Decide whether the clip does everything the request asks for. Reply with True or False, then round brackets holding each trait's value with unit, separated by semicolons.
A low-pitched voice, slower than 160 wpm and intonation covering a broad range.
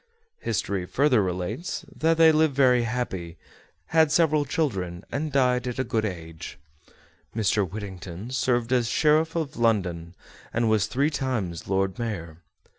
True (115 Hz; 145 wpm; 6.7 semitones)